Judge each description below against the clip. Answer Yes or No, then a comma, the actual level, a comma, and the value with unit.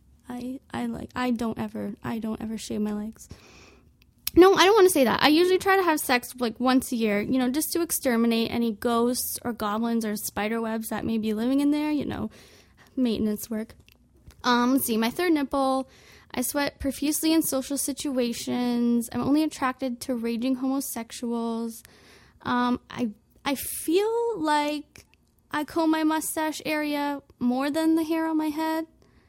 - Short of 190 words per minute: Yes, average, 175 wpm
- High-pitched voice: Yes, very high, 255 Hz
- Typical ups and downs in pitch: Yes, average, 4.5 semitones